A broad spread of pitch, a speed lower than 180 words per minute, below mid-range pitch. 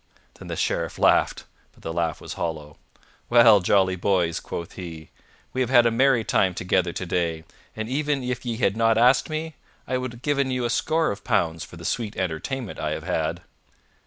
No: wide, 6.8 semitones; average, 195 wpm; low, 105 Hz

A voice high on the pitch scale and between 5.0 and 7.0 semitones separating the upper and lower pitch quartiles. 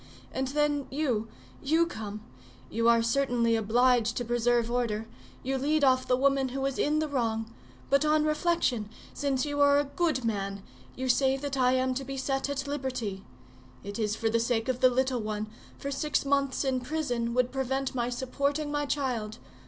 No: very high, 260 Hz; average, 3.2 semitones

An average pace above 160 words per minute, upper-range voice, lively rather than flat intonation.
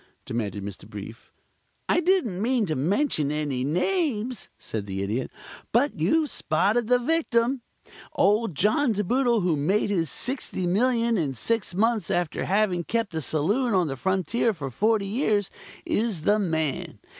No: average, 150 wpm; high, 200 Hz; wide, 7.2 semitones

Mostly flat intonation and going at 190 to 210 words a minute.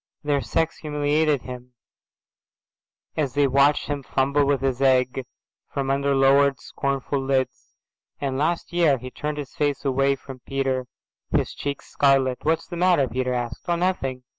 No: narrow, 1.9 semitones; average, 160 wpm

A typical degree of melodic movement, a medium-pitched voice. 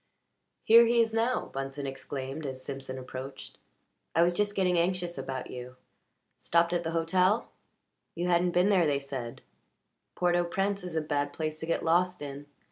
Yes: average, 4.7 semitones; medium, 170 Hz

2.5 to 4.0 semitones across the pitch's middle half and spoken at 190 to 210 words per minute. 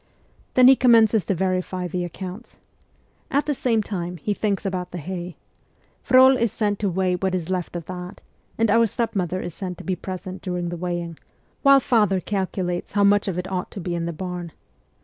Yes: average, 2.8 semitones; fast, 205 wpm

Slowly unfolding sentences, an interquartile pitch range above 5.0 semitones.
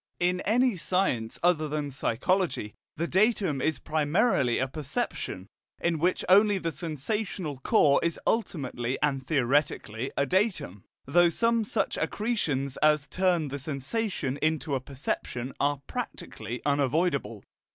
Yes: slow, 130 wpm; wide, 5.4 semitones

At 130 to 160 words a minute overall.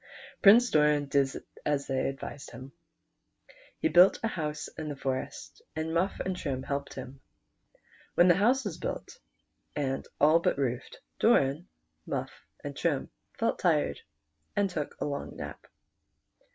Yes: average, 145 wpm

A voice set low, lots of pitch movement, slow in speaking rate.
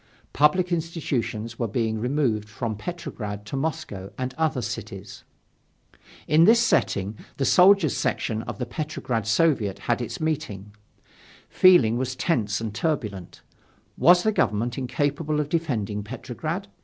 Yes: low, 130 Hz; wide, 6.4 semitones; slow, 130 wpm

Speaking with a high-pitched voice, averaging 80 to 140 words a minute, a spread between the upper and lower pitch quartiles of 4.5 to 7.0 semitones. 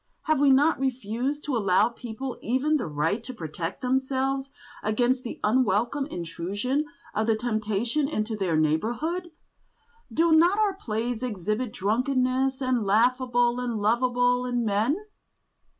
No: high, 245 Hz; slow, 135 wpm; average, 3.8 semitones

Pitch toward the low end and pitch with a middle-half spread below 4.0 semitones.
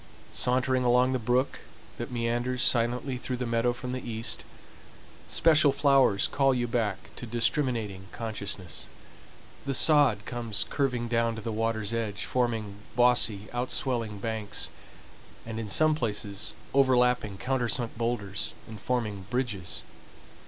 Yes: low, 120 Hz; narrow, 2.5 semitones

